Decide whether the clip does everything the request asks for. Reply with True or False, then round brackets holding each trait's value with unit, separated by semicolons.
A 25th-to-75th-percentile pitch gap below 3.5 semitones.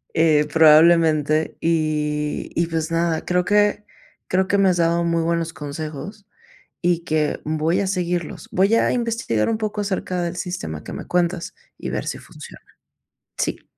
True (2.9 semitones)